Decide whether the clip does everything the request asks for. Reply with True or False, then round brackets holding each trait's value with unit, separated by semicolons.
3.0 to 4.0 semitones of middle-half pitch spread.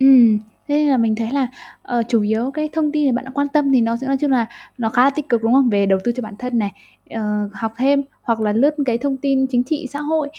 True (3.6 semitones)